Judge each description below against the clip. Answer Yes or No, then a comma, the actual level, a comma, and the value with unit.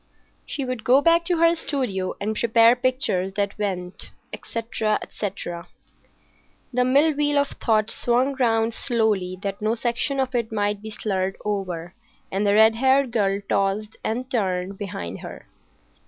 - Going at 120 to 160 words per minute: Yes, average, 155 wpm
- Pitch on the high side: Yes, high, 220 Hz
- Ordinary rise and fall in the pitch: Yes, average, 4.4 semitones